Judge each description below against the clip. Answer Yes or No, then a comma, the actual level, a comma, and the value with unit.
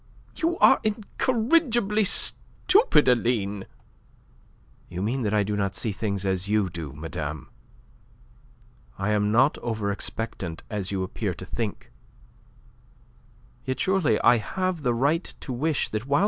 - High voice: No, low, 115 Hz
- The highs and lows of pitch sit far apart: Yes, wide, 8.5 semitones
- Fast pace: No, average, 140 wpm